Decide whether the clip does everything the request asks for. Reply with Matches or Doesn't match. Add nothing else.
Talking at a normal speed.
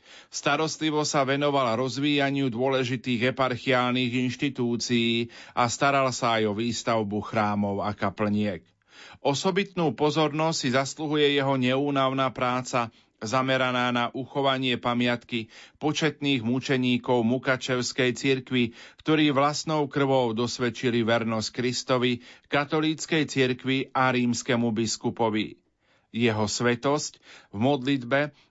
Doesn't match